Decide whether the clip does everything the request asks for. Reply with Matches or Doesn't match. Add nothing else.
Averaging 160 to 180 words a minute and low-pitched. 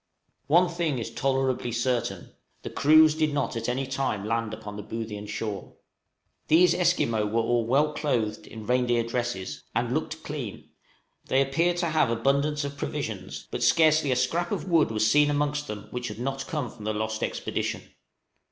Matches